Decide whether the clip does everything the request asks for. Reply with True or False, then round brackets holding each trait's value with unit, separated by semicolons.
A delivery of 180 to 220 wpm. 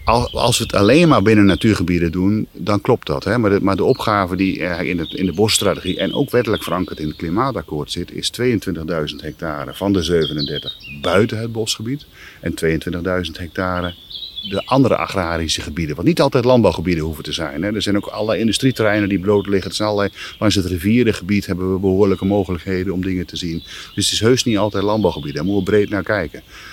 True (200 wpm)